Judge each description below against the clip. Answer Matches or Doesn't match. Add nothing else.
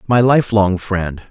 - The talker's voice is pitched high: Doesn't match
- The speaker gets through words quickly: Doesn't match